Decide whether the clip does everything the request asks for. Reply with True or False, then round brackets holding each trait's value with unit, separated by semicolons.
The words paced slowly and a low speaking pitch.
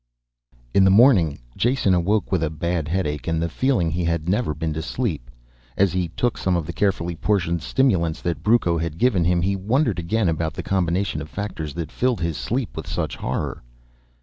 False (200 wpm; 85 Hz)